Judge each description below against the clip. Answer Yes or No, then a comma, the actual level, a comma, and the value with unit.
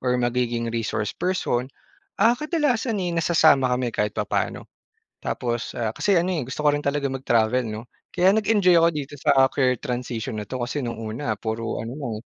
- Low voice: Yes, low, 130 Hz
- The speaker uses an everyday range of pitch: No, wide, 6.1 semitones